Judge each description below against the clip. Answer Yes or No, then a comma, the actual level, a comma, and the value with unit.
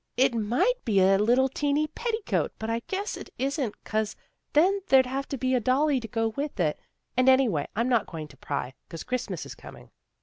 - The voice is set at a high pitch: Yes, very high, 255 Hz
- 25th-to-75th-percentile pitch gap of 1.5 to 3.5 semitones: No, average, 4.5 semitones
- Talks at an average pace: No, fast, 210 wpm